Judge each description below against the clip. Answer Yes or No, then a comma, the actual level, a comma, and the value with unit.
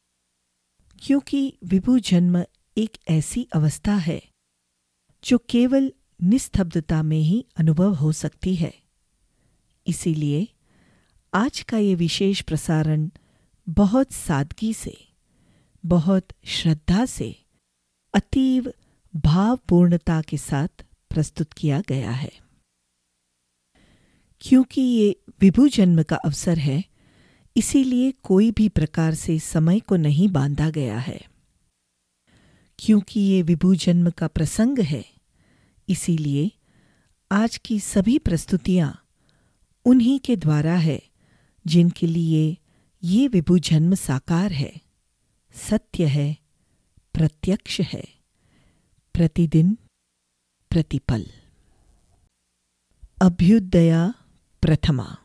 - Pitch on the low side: No, medium, 170 Hz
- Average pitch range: No, wide, 5.7 semitones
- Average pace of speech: No, slow, 90 wpm